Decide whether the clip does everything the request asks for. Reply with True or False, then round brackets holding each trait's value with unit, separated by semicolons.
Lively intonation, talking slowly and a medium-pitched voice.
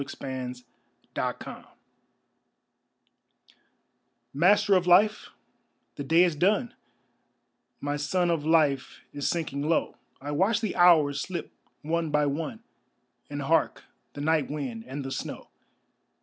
False (3.9 semitones; 120 wpm; 155 Hz)